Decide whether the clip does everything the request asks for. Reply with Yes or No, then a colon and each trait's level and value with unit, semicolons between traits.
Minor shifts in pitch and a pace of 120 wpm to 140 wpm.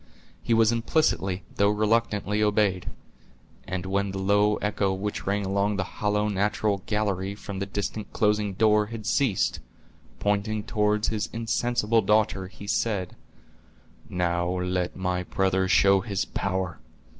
Yes: narrow, 2.0 semitones; slow, 135 wpm